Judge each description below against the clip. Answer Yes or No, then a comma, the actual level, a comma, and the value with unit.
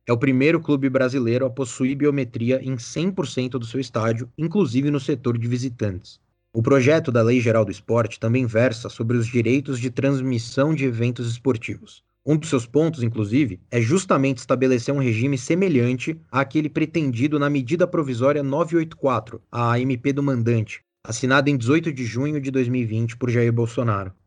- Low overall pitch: Yes, low, 130 Hz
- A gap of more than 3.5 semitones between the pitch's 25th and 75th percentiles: No, average, 3.2 semitones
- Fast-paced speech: No, average, 165 wpm